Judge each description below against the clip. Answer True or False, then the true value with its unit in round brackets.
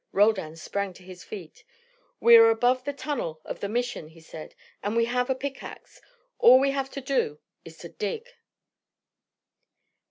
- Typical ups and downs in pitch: False (7.0 semitones)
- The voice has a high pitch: True (235 Hz)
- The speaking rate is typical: True (165 wpm)